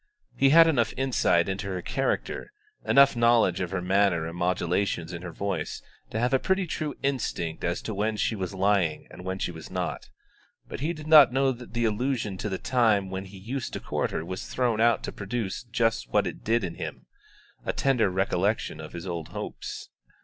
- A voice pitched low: Yes, low, 100 Hz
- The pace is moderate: No, fast, 210 wpm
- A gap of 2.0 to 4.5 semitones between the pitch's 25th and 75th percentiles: No, average, 5.2 semitones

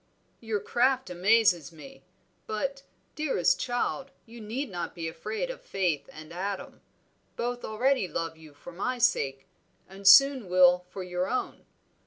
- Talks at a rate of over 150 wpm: No, average, 145 wpm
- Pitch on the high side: Yes, high, 200 Hz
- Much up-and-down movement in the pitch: Yes, wide, 5.8 semitones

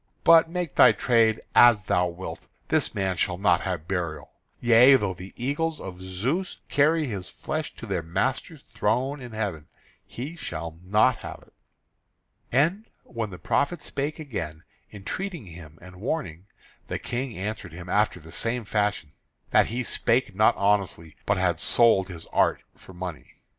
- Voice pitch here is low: Yes, low, 105 Hz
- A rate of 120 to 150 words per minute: No, average, 160 wpm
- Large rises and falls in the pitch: Yes, wide, 6.3 semitones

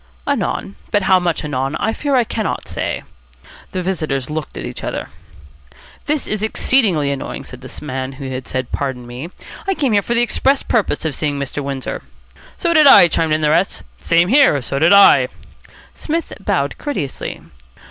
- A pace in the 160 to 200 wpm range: Yes, average, 180 wpm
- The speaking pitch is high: No, medium, 165 Hz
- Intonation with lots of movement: Yes, wide, 8.3 semitones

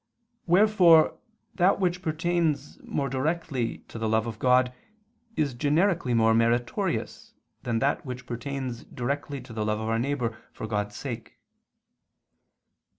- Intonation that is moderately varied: No, wide, 5.8 semitones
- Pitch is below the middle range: Yes, low, 130 Hz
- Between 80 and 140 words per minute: Yes, slow, 135 wpm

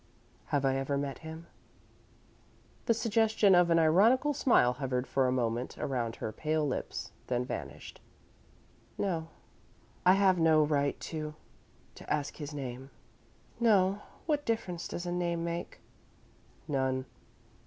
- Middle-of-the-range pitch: Yes, medium, 160 Hz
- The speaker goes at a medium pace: No, slow, 130 wpm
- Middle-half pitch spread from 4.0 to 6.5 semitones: Yes, wide, 5.5 semitones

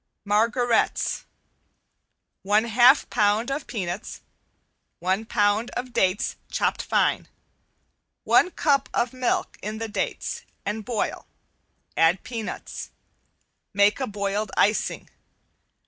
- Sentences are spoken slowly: Yes, slow, 100 wpm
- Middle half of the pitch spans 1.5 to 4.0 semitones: Yes, average, 2.9 semitones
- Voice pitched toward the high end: Yes, high, 215 Hz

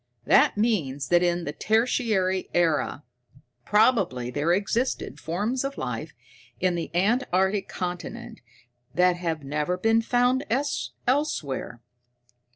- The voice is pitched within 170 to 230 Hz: Yes, medium, 185 Hz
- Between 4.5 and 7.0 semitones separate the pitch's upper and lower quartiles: Yes, average, 5.2 semitones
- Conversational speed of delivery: No, slow, 110 wpm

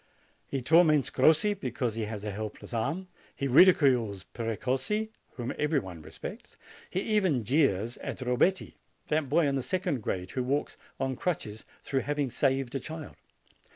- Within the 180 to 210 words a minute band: No, average, 155 wpm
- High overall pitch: No, low, 135 Hz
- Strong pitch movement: No, average, 5.0 semitones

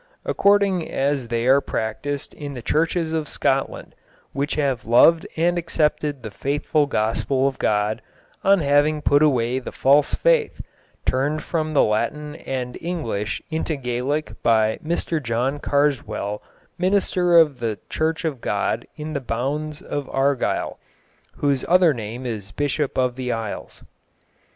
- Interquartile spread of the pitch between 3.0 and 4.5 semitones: Yes, average, 4.2 semitones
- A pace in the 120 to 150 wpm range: Yes, average, 140 wpm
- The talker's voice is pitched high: No, medium, 140 Hz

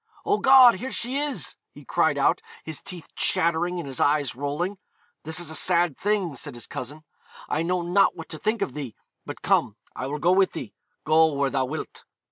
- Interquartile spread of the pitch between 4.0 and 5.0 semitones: Yes, average, 4.6 semitones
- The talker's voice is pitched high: No, medium, 165 Hz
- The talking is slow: No, fast, 205 wpm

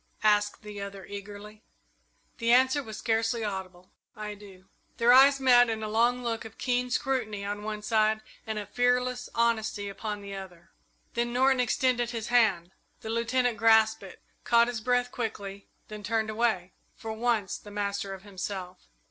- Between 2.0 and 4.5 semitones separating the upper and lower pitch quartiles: Yes, average, 2.9 semitones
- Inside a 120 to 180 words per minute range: Yes, average, 165 wpm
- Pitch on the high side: Yes, high, 220 Hz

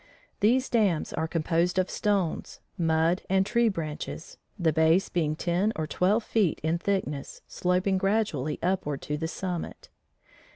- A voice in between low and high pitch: Yes, medium, 175 Hz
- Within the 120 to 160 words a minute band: Yes, average, 140 wpm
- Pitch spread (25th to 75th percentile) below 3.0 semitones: No, average, 3.4 semitones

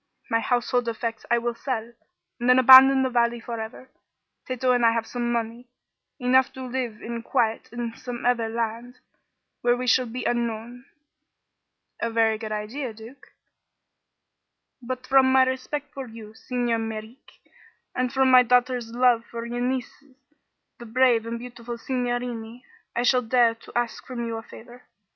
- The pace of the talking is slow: No, average, 160 wpm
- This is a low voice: No, high, 240 Hz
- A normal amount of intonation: No, narrow, 1.7 semitones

